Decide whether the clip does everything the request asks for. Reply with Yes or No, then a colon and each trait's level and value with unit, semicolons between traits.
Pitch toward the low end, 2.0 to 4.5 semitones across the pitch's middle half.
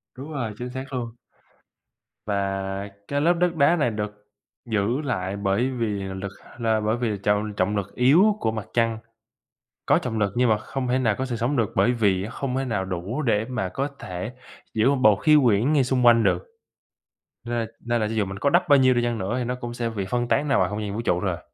Yes: low, 115 Hz; average, 3.9 semitones